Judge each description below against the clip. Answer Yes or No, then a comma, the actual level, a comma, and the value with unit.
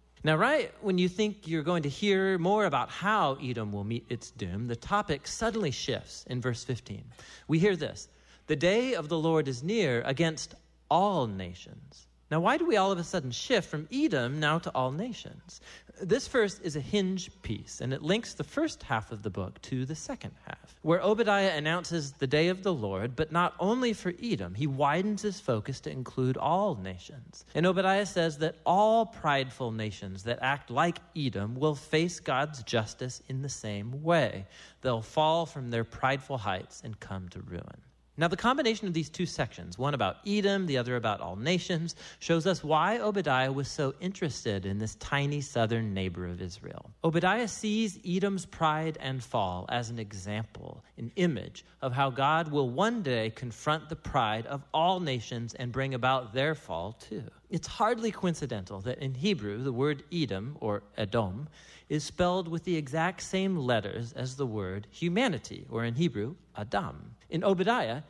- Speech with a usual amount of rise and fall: No, wide, 7.2 semitones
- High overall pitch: No, medium, 145 Hz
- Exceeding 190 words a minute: No, average, 180 wpm